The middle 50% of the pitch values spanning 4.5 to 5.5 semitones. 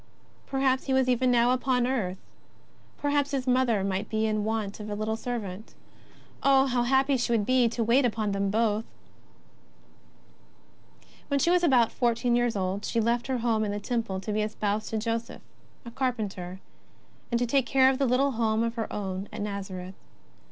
No: average, 3.4 semitones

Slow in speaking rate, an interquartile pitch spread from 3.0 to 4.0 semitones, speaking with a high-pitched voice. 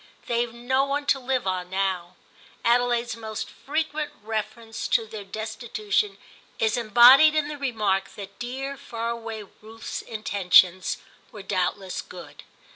Yes: slow, 130 wpm; average, 3.4 semitones; high, 225 Hz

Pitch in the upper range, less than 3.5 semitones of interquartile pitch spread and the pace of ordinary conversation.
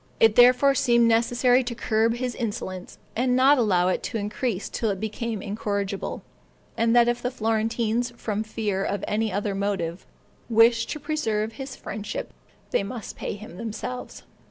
Yes: high, 225 Hz; average, 2.8 semitones; average, 160 wpm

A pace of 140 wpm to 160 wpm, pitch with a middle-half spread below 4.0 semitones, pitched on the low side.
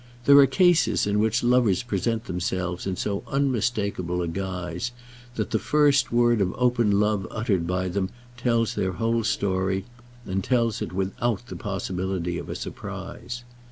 No: average, 155 wpm; average, 4.3 semitones; low, 105 Hz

